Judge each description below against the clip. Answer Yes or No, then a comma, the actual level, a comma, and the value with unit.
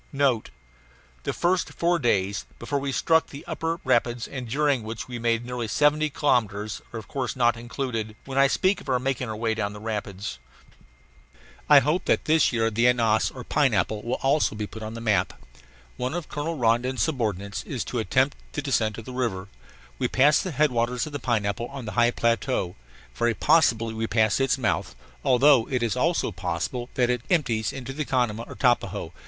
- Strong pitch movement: No, average, 3.8 semitones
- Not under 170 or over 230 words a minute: Yes, average, 195 wpm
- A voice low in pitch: Yes, low, 120 Hz